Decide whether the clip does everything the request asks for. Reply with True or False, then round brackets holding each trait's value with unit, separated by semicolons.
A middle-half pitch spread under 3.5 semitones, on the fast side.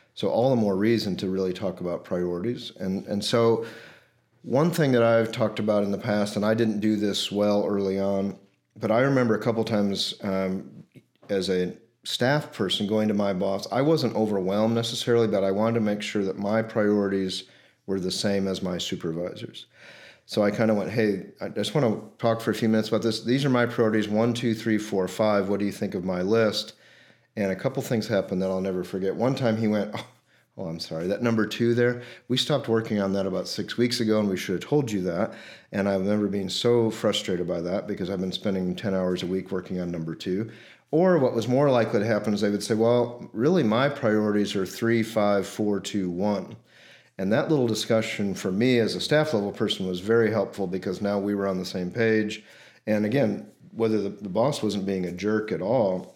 True (2.7 semitones; 225 wpm)